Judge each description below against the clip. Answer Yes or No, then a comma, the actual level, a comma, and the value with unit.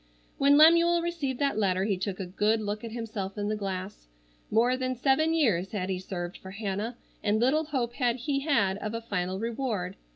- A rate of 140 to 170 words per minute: No, average, 200 wpm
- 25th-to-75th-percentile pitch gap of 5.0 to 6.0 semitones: Yes, wide, 5.5 semitones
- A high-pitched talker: Yes, high, 220 Hz